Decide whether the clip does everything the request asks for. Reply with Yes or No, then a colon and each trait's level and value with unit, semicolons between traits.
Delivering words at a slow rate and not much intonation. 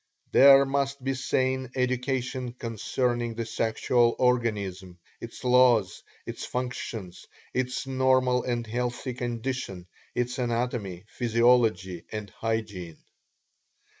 Yes: slow, 100 wpm; narrow, 2.3 semitones